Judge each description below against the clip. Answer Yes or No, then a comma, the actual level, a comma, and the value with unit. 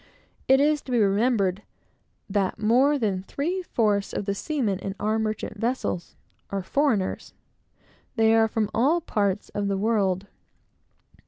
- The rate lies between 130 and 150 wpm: Yes, average, 145 wpm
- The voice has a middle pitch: No, high, 215 Hz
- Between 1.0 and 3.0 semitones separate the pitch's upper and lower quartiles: No, average, 4.3 semitones